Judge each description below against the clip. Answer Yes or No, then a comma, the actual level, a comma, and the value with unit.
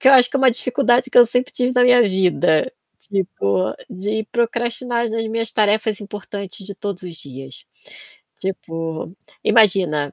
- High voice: Yes, high, 210 Hz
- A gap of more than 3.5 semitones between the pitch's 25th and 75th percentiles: Yes, average, 4.9 semitones